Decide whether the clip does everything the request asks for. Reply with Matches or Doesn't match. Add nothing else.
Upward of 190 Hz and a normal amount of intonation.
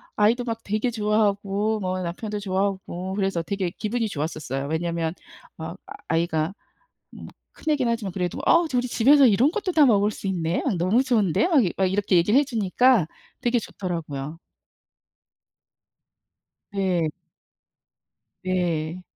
Matches